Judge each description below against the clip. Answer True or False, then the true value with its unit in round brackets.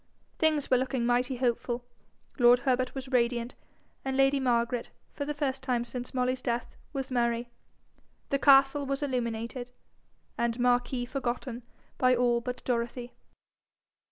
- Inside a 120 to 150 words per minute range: True (135 wpm)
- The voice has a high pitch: True (250 Hz)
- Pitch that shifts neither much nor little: False (1.8 semitones)